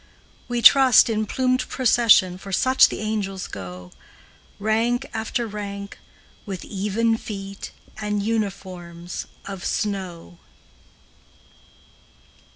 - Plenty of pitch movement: No, average, 3.1 semitones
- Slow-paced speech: Yes, slow, 95 wpm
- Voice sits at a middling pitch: No, high, 205 Hz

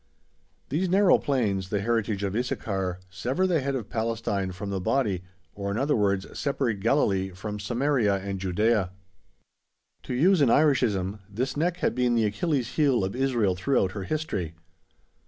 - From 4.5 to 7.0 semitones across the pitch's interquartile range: Yes, wide, 5.6 semitones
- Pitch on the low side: Yes, low, 110 Hz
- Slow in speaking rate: No, average, 160 wpm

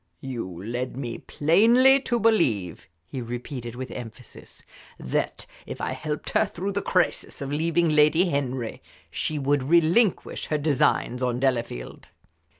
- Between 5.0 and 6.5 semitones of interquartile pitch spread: Yes, wide, 5.5 semitones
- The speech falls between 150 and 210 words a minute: No, average, 140 wpm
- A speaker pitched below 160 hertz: Yes, medium, 140 Hz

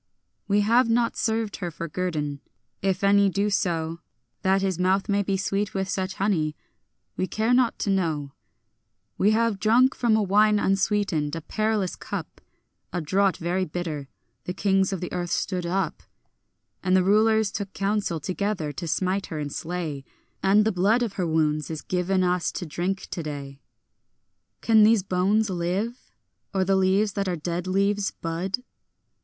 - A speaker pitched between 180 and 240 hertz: Yes, high, 190 Hz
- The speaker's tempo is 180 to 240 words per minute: No, average, 165 wpm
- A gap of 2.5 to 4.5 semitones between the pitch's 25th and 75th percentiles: Yes, average, 3.0 semitones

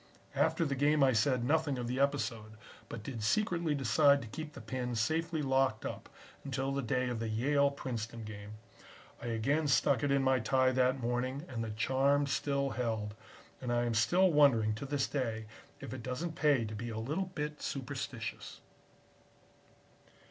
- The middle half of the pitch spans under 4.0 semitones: Yes, average, 3.6 semitones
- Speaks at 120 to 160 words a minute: No, average, 175 wpm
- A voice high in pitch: No, low, 130 Hz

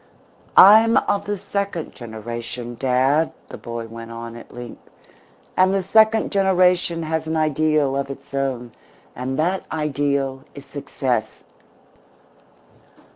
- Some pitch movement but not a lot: No, wide, 6.6 semitones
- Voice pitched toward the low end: No, medium, 145 Hz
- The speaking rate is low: Yes, slow, 125 wpm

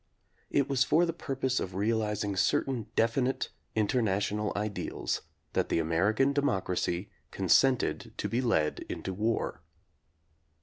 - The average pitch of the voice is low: Yes, low, 110 Hz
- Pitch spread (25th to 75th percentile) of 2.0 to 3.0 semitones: No, average, 4.7 semitones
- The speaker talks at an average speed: No, slow, 120 wpm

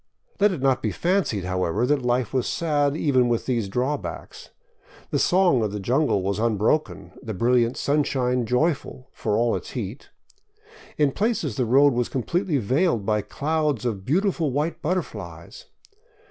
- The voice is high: No, low, 130 Hz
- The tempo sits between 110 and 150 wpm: No, average, 160 wpm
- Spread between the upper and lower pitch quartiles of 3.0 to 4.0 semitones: No, average, 4.7 semitones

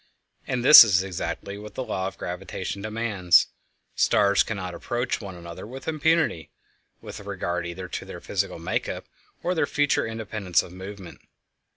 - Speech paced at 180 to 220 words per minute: No, average, 160 wpm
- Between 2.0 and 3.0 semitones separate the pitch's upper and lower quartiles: No, average, 4.2 semitones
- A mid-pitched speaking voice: No, low, 100 Hz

